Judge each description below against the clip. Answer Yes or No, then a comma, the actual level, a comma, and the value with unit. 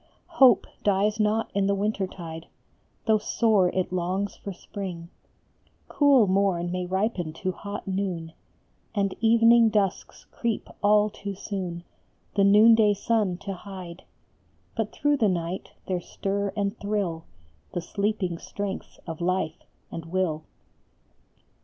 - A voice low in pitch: No, high, 195 Hz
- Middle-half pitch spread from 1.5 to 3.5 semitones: Yes, average, 2.8 semitones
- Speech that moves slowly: Yes, slow, 130 wpm